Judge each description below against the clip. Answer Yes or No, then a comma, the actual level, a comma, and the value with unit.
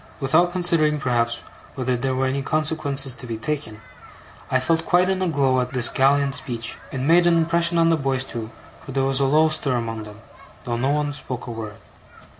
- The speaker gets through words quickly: Yes, fast, 210 wpm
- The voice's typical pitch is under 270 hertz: Yes, low, 135 Hz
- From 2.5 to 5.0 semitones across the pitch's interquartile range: Yes, average, 3.9 semitones